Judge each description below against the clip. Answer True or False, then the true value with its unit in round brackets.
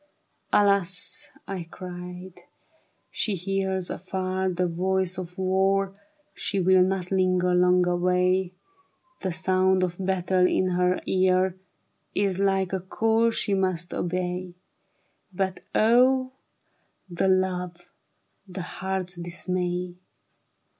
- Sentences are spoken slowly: True (115 wpm)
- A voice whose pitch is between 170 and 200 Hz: True (185 Hz)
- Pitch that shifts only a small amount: True (1.1 semitones)